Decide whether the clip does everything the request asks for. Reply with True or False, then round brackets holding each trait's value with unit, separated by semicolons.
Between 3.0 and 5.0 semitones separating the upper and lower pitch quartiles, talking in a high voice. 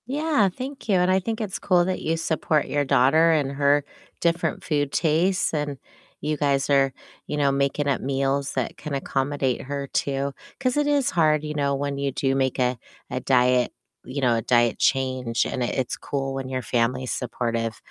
False (3.3 semitones; 140 Hz)